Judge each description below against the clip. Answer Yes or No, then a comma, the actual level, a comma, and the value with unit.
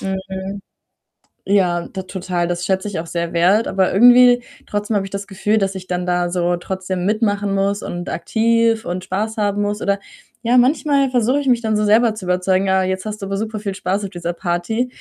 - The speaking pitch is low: No, high, 195 Hz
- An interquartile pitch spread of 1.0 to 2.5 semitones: No, average, 2.9 semitones